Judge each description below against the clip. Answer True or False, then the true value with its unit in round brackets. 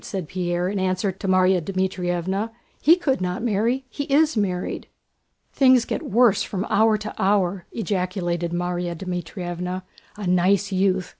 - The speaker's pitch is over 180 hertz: True (190 Hz)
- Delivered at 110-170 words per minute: True (140 wpm)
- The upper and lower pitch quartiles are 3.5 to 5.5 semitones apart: False (2.9 semitones)